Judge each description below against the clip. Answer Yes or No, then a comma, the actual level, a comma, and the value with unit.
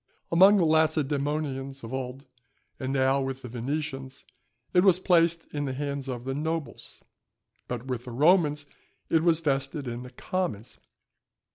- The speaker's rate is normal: Yes, average, 150 wpm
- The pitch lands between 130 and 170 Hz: Yes, medium, 140 Hz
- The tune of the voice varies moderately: Yes, average, 3.3 semitones